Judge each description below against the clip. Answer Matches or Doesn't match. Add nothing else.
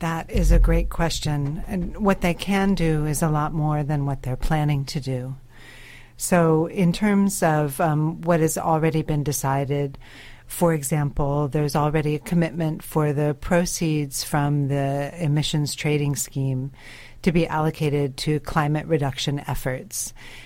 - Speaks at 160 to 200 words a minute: Doesn't match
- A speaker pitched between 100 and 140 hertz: Doesn't match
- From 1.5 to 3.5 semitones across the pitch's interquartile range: Matches